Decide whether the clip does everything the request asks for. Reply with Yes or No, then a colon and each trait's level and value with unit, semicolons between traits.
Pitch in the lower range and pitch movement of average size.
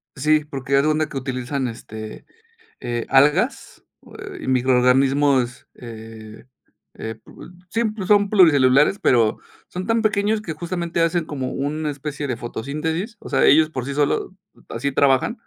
No: medium, 145 Hz; average, 5.0 semitones